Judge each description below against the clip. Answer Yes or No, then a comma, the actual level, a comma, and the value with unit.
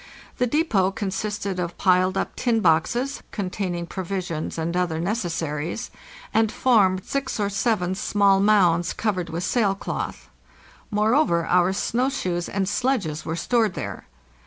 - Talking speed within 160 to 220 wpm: No, average, 140 wpm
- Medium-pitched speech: No, high, 195 Hz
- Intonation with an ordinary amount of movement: Yes, average, 3.9 semitones